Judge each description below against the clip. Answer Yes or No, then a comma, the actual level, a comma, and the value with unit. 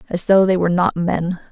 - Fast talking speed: Yes, fast, 235 wpm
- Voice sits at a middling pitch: Yes, medium, 180 Hz